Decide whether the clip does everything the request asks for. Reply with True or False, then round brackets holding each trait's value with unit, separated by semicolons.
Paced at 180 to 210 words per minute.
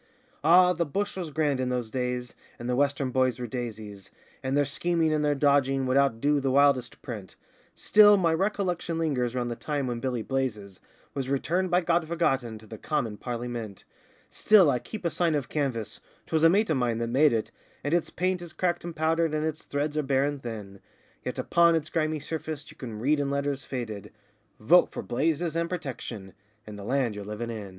True (205 wpm)